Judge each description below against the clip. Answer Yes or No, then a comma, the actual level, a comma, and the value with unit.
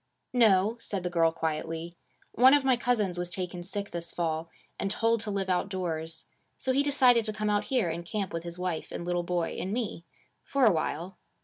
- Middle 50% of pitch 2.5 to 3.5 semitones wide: No, average, 4.6 semitones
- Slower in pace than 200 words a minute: No, fast, 205 wpm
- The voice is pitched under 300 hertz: Yes, medium, 185 Hz